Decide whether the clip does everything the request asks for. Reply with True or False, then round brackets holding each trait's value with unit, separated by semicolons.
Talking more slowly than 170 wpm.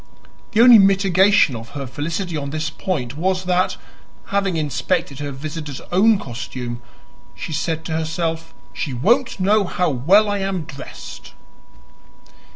True (140 wpm)